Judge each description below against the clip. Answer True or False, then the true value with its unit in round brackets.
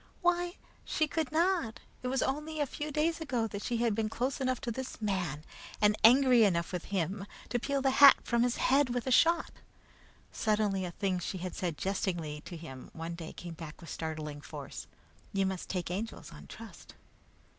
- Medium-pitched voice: False (220 Hz)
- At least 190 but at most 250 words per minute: True (195 wpm)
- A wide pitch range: True (6.9 semitones)